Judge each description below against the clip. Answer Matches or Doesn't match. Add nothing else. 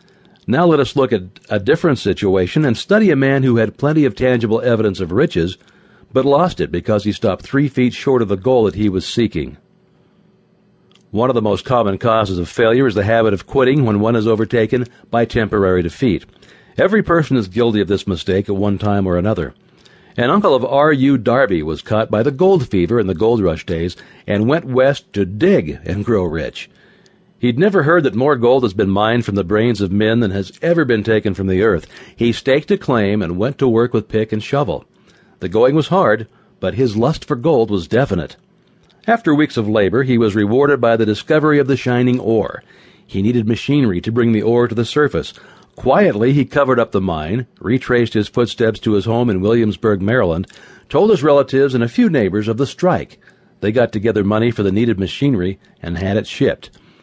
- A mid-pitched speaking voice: Doesn't match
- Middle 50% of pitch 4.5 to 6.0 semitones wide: Matches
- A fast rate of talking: Matches